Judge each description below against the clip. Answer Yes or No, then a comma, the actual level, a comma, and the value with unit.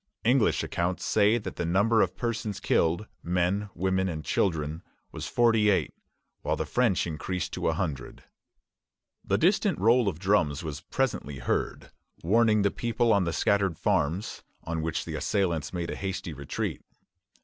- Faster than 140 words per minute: Yes, average, 160 wpm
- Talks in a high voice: No, very low, 95 Hz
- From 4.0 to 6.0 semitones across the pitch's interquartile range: Yes, average, 4.6 semitones